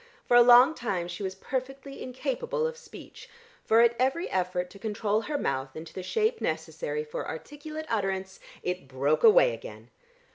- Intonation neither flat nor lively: No, wide, 8.0 semitones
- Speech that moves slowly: No, average, 170 wpm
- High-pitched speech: Yes, high, 230 Hz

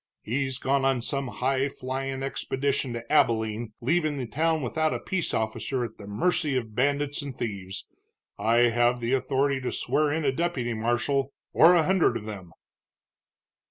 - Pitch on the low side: Yes, low, 130 Hz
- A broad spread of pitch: No, average, 3.4 semitones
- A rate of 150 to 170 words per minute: Yes, average, 165 wpm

